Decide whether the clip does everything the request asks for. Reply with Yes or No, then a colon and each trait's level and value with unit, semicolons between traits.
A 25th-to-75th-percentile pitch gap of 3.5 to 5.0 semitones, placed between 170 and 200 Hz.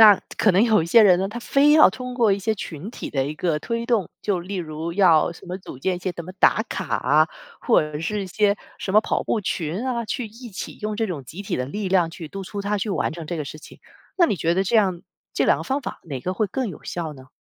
Yes: average, 4.7 semitones; high, 190 Hz